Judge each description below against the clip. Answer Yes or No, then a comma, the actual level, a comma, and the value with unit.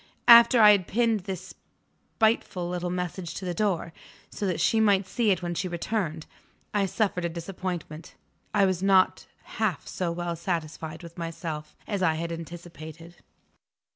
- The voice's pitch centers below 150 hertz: No, medium, 180 Hz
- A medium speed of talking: Yes, average, 160 wpm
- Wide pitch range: No, average, 2.8 semitones